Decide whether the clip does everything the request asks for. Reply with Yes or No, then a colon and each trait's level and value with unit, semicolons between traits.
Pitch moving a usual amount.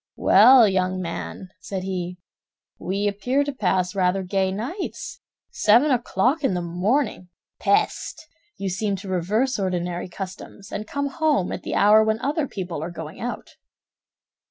Yes: average, 5.0 semitones